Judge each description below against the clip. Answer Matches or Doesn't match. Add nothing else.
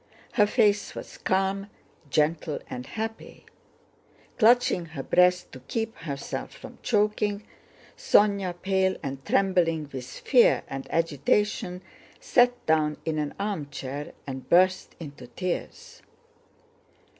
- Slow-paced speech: Matches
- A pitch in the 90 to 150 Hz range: Doesn't match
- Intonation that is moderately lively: Doesn't match